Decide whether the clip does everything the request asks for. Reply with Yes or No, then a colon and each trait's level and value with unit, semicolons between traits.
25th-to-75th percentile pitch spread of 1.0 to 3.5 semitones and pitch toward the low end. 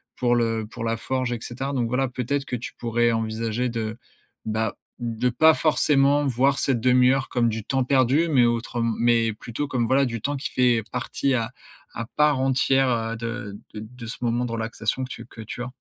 Yes: narrow, 2.5 semitones; low, 120 Hz